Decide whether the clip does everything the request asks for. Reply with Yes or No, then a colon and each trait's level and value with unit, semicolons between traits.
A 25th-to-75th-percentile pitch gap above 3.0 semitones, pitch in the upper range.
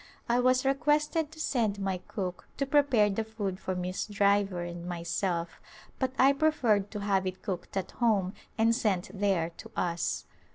Yes: average, 5.0 semitones; high, 205 Hz